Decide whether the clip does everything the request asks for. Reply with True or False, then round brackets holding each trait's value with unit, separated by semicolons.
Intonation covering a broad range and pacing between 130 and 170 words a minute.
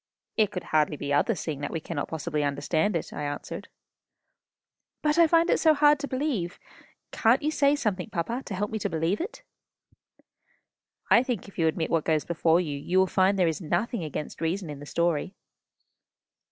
False (6.9 semitones; 190 wpm)